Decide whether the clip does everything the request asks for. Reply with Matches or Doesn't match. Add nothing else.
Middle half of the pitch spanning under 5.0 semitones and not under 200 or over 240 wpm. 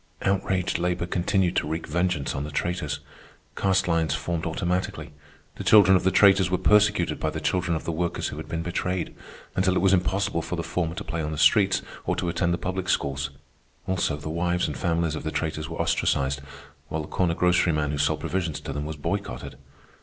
Matches